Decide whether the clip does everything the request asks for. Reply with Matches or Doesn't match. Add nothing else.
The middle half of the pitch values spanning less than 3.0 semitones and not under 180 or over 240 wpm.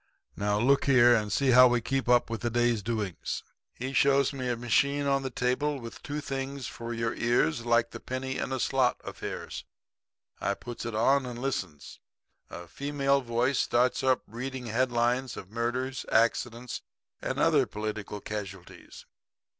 Doesn't match